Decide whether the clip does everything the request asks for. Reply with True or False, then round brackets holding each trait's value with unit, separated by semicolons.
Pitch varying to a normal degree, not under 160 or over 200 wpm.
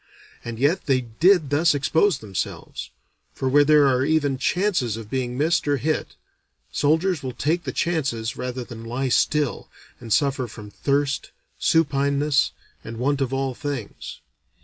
False (3.5 semitones; 150 wpm)